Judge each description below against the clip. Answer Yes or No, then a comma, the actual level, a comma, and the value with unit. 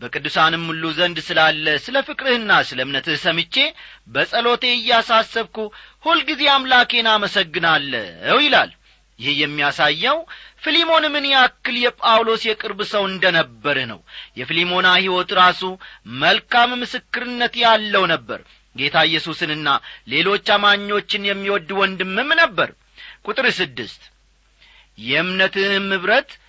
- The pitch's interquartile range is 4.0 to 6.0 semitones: No, wide, 6.8 semitones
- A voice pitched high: Yes, high, 195 Hz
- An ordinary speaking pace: Yes, average, 100 wpm